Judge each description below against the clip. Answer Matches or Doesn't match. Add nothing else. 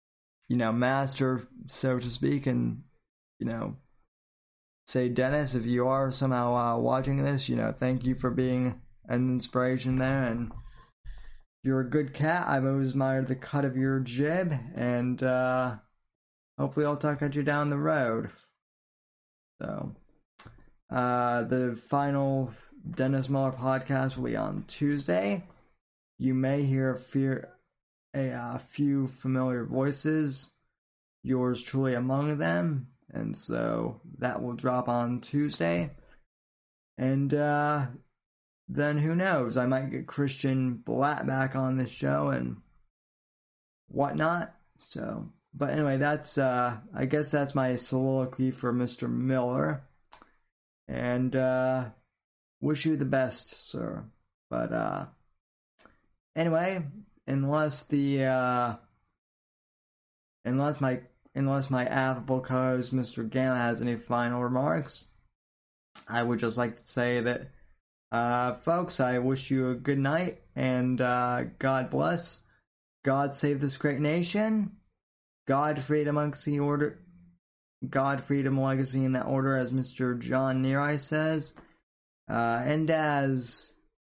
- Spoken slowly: Matches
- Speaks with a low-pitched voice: Matches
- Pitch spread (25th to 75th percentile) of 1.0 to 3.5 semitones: Matches